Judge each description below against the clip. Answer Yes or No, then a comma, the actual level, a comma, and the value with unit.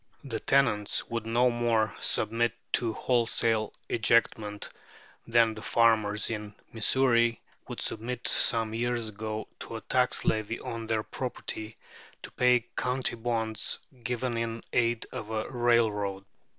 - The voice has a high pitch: No, low, 115 Hz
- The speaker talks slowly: Yes, slow, 130 wpm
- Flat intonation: Yes, narrow, 1.6 semitones